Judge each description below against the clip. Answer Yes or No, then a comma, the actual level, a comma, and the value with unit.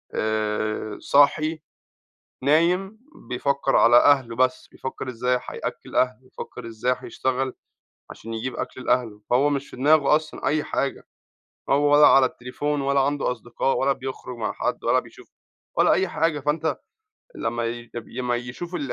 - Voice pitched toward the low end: Yes, low, 130 Hz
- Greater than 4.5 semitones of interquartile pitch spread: No, average, 3.2 semitones